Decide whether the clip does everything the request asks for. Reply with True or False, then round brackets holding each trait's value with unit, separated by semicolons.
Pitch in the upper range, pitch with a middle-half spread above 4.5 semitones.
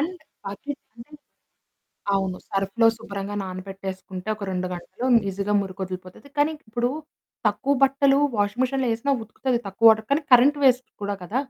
True (215 Hz; 5.2 semitones)